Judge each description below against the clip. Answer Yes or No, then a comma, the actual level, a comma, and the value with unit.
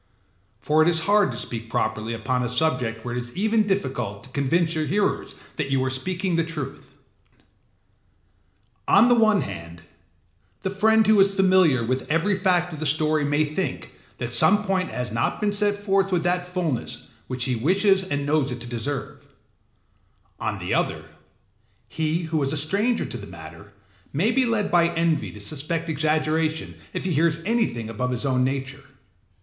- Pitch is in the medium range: Yes, medium, 155 Hz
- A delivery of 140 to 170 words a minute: No, average, 180 wpm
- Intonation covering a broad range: Yes, wide, 6.8 semitones